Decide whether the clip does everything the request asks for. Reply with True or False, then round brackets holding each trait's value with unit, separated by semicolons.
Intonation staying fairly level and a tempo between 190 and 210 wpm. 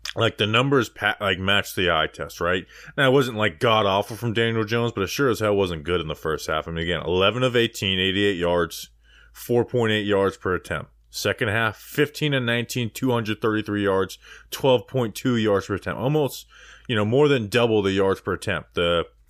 False (3.7 semitones; 200 wpm)